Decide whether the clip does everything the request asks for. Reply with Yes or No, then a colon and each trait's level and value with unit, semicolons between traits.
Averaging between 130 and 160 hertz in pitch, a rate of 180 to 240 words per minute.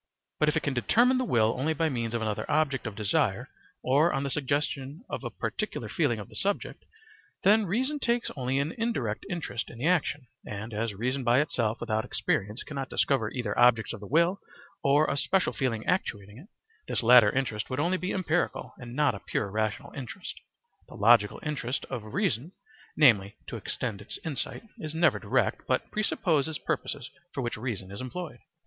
Yes: low, 135 Hz; average, 190 wpm